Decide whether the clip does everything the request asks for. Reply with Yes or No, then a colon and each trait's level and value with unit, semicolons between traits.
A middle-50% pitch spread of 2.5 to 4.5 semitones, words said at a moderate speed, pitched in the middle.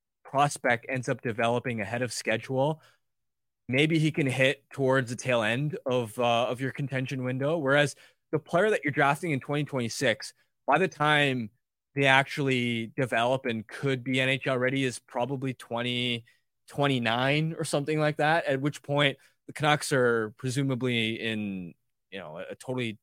No: average, 3.0 semitones; average, 160 wpm; low, 130 Hz